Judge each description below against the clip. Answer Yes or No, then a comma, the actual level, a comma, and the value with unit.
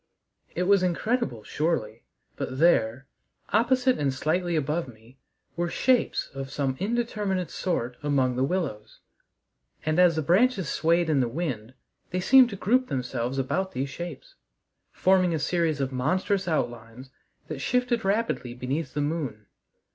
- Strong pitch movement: Yes, wide, 6.3 semitones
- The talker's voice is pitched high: No, medium, 160 Hz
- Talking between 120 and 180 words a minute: Yes, average, 145 wpm